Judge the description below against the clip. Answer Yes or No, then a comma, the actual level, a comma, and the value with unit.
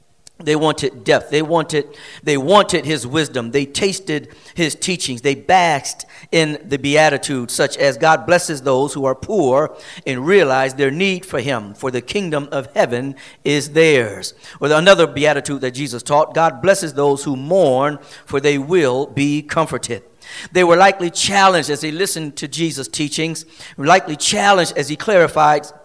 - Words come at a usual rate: Yes, average, 165 wpm